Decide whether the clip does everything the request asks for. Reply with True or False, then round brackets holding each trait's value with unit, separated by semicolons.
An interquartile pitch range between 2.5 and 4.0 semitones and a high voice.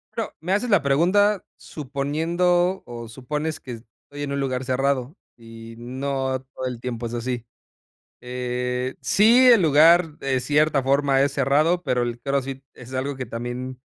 False (3.6 semitones; 135 Hz)